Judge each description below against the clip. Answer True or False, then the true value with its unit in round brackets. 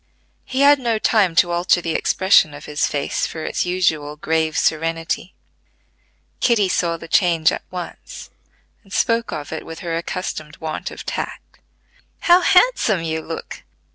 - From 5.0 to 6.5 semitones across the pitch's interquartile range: False (3.8 semitones)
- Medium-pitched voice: True (170 Hz)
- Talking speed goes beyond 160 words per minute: False (155 wpm)